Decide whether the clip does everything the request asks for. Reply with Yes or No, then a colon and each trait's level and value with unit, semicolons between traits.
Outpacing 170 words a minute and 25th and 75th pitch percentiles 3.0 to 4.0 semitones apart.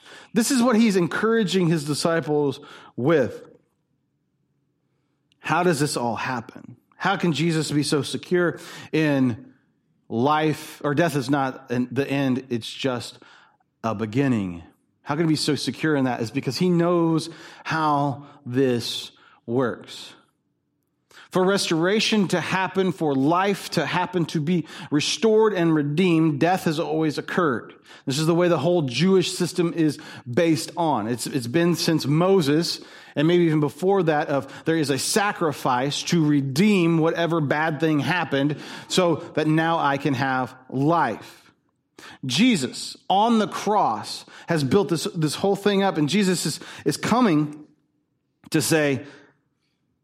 No: average, 145 wpm; average, 3.4 semitones